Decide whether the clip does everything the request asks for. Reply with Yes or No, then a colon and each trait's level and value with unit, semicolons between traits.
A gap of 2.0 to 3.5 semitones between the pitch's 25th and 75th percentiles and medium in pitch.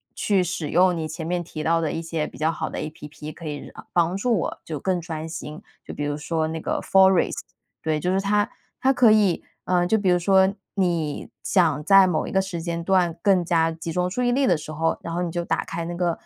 Yes: average, 2.9 semitones; medium, 170 Hz